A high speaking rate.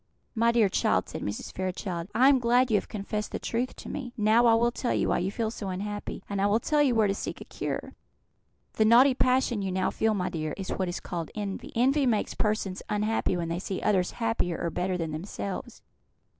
Yes: fast, 225 wpm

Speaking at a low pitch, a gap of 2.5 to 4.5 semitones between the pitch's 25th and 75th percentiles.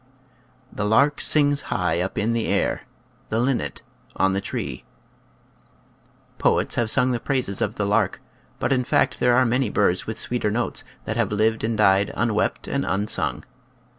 Yes: low, 115 Hz; average, 3.4 semitones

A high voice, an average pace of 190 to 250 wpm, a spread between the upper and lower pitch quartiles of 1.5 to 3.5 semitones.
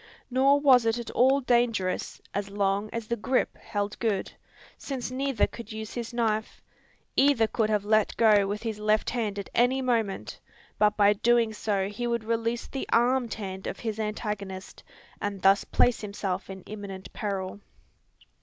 No: high, 220 Hz; average, 165 wpm; average, 2.8 semitones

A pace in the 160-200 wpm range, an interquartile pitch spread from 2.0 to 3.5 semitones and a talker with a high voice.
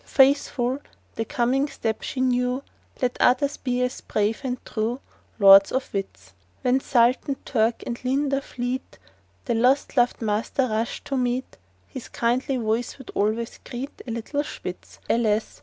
No: average, 150 wpm; narrow, 2.5 semitones; high, 245 Hz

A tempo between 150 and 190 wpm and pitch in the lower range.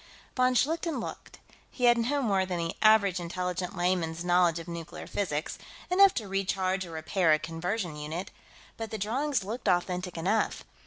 No: average, 165 wpm; medium, 185 Hz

